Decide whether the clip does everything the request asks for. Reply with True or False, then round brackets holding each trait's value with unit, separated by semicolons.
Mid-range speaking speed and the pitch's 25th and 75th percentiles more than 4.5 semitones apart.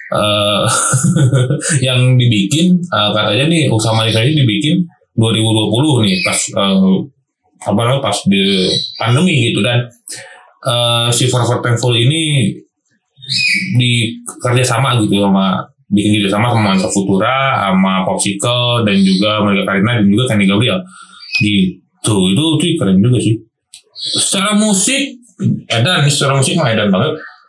True (130 wpm; 4.9 semitones)